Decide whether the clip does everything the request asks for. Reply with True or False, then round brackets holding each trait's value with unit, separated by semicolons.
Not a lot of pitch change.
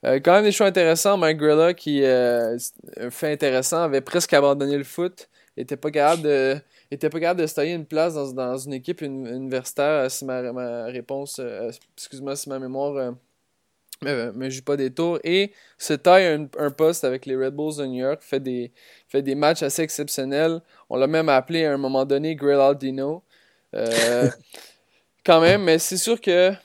False (3.5 semitones)